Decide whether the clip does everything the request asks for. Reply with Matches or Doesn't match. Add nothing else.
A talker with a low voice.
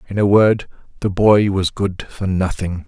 Matches